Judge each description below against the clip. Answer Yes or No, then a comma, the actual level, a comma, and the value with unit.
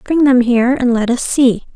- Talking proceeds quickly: Yes, fast, 240 wpm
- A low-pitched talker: No, very high, 250 Hz